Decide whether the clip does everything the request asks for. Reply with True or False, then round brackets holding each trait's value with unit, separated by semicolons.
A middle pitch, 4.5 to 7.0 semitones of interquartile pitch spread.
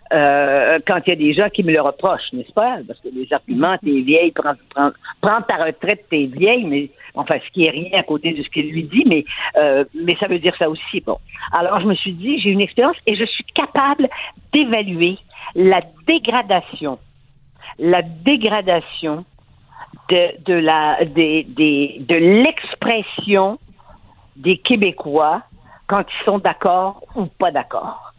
True (175 Hz; 5.3 semitones)